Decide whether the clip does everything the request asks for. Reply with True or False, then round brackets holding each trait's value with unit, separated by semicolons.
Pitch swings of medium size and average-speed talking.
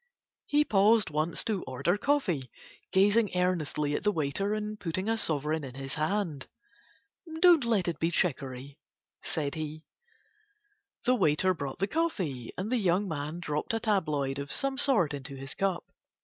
False (6.2 semitones; 160 wpm)